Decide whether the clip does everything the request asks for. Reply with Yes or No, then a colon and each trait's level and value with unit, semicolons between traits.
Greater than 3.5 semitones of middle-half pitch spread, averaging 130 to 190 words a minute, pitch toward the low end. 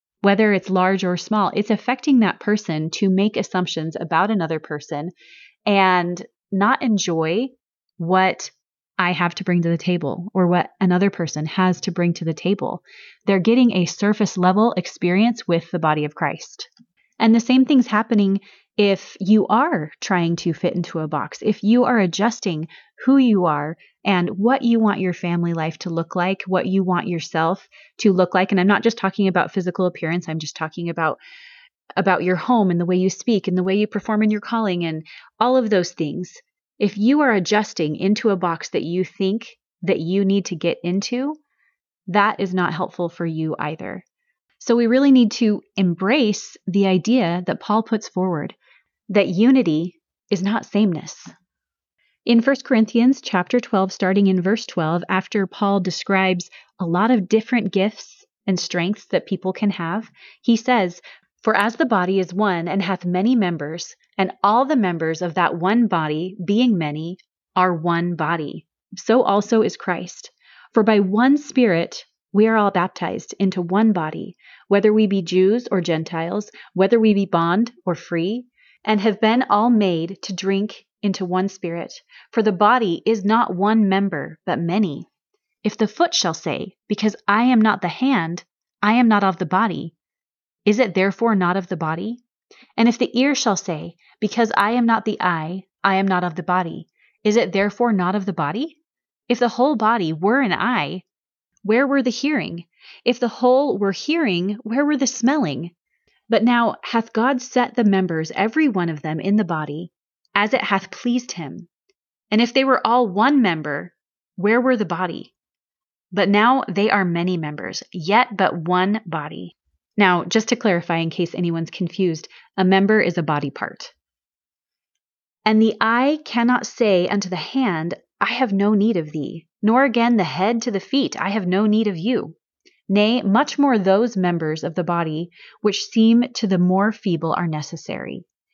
No: average, 4.4 semitones; average, 180 wpm; high, 195 Hz